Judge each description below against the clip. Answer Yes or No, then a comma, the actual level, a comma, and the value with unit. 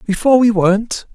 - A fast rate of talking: No, average, 160 wpm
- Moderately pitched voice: No, high, 215 Hz